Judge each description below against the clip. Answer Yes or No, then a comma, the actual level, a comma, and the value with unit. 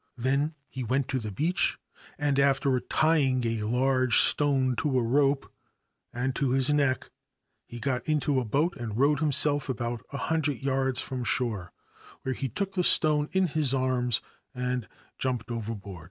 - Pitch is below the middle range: Yes, low, 130 Hz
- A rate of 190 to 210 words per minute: No, average, 165 wpm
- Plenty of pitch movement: No, average, 2.8 semitones